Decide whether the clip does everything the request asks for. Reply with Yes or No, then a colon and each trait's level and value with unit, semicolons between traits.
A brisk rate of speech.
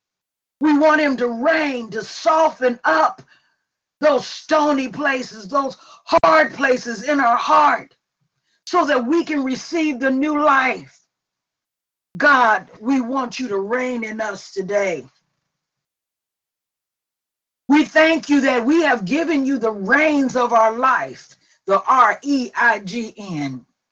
No: slow, 135 wpm